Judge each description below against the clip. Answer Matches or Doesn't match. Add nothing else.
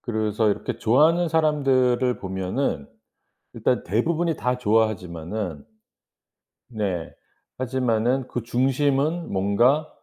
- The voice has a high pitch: Doesn't match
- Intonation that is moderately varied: Matches